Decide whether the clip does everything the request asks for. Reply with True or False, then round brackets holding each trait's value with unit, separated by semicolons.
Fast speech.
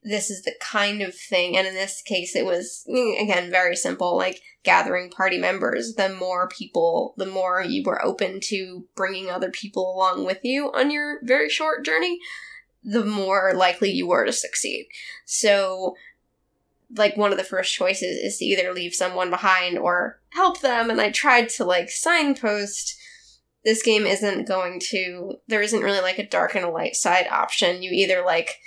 False (180 wpm)